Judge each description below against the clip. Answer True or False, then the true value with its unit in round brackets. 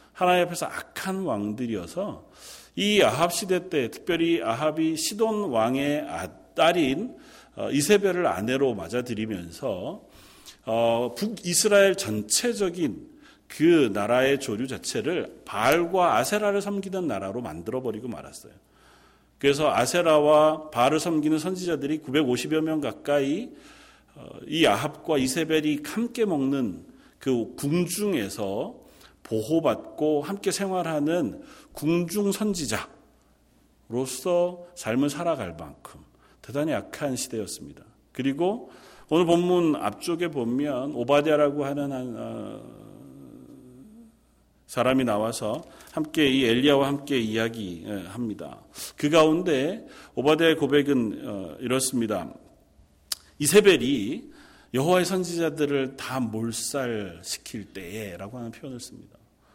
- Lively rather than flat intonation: True (6.3 semitones)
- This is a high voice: False (150 Hz)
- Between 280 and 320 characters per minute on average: False (245 characters per minute)